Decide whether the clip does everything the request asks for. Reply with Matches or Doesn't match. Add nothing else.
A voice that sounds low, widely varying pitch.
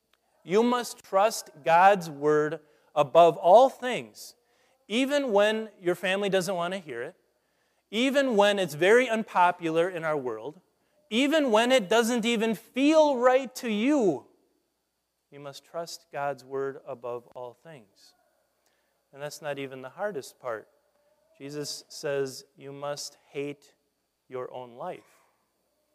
Doesn't match